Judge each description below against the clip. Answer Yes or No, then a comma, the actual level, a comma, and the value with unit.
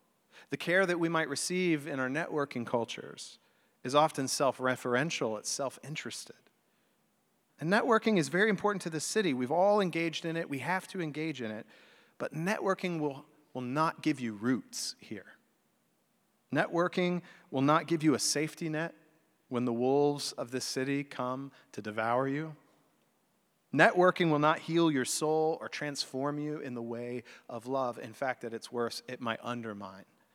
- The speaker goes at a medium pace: Yes, average, 165 wpm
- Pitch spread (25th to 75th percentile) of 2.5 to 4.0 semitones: No, average, 4.6 semitones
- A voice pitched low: No, medium, 150 Hz